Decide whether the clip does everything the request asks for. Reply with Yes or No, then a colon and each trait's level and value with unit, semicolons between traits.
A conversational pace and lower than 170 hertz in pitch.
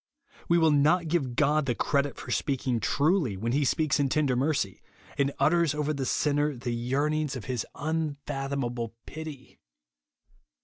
Yes: average, 160 wpm; medium, 140 Hz